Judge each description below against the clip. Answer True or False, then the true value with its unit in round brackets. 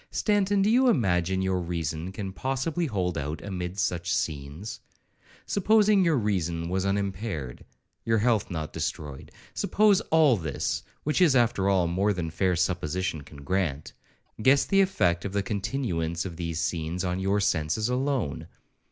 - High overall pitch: False (95 Hz)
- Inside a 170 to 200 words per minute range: False (145 wpm)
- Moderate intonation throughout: False (6.6 semitones)